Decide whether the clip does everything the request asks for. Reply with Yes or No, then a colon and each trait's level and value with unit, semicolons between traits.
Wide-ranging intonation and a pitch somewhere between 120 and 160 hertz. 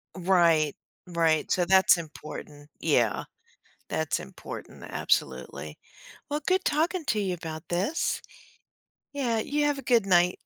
No: wide, 8.8 semitones; medium, 185 Hz